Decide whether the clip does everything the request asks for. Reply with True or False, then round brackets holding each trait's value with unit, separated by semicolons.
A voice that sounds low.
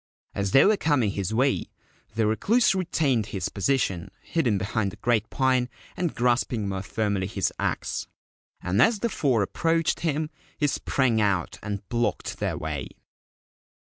True (115 Hz)